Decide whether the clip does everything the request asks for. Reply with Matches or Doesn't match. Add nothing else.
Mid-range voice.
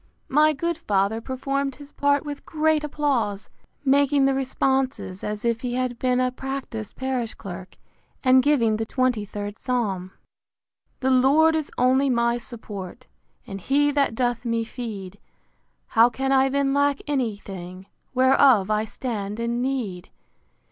Doesn't match